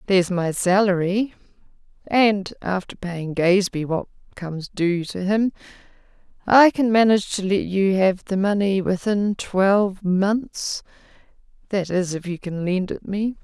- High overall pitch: Yes, high, 195 Hz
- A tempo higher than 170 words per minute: No, average, 140 wpm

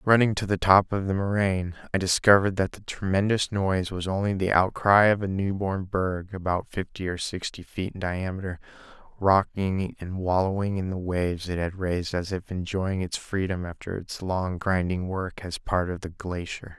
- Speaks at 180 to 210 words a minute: Yes, average, 185 wpm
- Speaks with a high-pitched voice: No, very low, 95 Hz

